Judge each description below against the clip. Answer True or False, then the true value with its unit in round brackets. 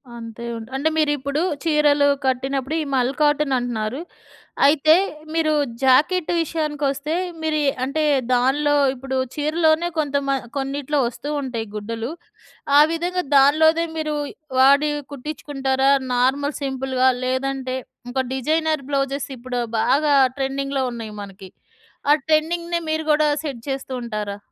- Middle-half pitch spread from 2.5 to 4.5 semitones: True (2.9 semitones)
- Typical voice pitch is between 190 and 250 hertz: False (275 Hz)